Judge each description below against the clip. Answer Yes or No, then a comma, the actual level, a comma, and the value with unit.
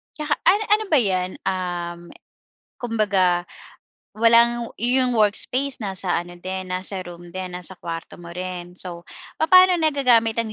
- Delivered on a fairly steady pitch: No, average, 5.2 semitones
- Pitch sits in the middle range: No, high, 195 Hz